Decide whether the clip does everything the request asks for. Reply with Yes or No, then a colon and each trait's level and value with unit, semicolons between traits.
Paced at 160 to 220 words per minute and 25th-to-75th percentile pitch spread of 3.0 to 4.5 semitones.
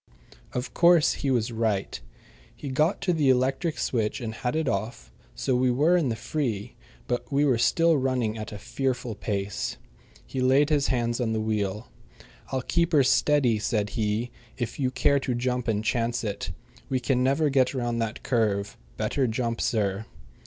Yes: average, 180 wpm; average, 3.6 semitones